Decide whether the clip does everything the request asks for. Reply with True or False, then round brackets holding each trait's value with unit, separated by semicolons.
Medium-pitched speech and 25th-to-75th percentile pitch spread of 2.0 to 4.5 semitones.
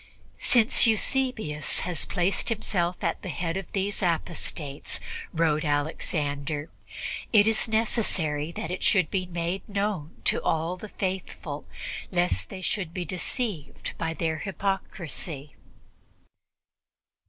True (175 Hz; 4.1 semitones)